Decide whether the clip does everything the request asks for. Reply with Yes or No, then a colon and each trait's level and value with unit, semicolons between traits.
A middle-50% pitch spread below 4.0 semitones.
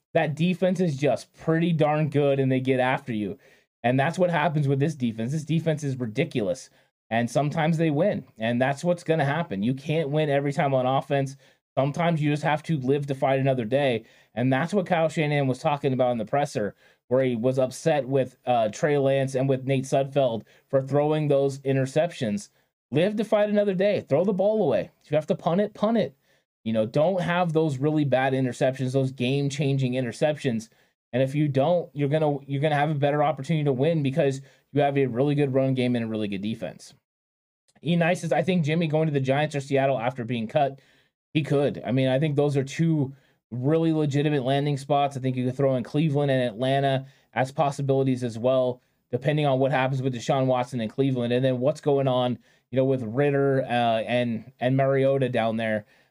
Yes: average, 2.8 semitones